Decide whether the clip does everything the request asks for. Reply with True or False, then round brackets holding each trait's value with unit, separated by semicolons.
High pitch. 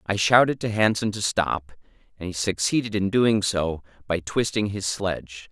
False (100 Hz)